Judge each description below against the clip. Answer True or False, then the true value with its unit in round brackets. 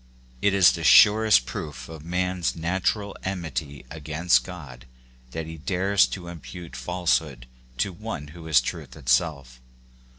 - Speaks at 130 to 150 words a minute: True (140 wpm)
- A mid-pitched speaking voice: False (80 Hz)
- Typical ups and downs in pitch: True (4.2 semitones)